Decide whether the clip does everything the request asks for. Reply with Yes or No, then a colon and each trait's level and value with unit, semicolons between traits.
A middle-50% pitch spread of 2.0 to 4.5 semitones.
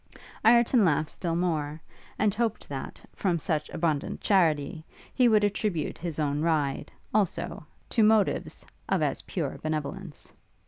No: wide, 5.5 semitones